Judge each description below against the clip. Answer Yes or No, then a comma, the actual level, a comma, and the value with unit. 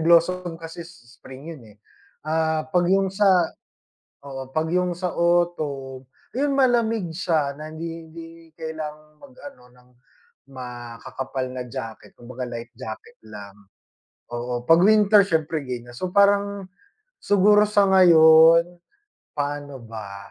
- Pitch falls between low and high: Yes, medium, 160 Hz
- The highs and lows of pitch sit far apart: Yes, wide, 5.9 semitones